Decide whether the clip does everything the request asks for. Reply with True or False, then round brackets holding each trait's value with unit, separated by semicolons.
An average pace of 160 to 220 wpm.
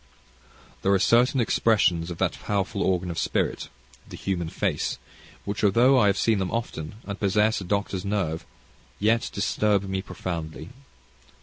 False (150 wpm)